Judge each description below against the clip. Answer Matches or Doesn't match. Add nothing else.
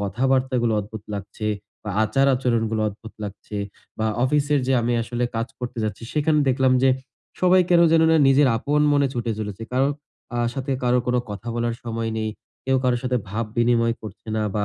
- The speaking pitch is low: Matches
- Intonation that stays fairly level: Doesn't match